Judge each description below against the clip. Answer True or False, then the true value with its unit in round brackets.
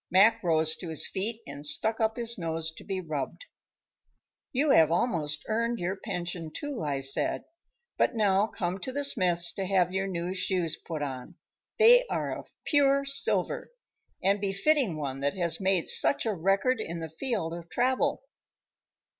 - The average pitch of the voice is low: False (190 Hz)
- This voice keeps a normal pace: True (170 wpm)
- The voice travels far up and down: True (5.9 semitones)